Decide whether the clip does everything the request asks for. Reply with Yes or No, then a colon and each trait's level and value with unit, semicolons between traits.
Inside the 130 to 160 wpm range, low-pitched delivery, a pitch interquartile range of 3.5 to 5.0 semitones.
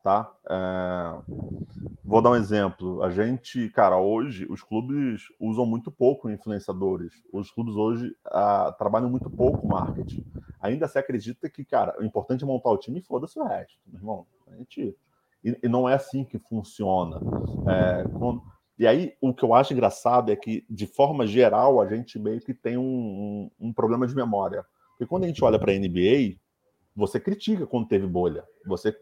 No: average, 180 wpm; low, 110 Hz; average, 4.0 semitones